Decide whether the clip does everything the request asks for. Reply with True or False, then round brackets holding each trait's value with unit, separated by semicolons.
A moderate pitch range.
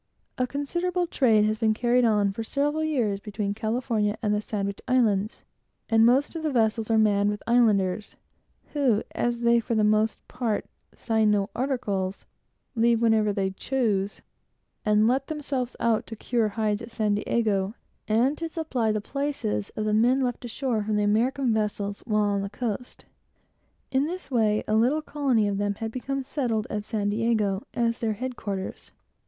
True (3.2 semitones)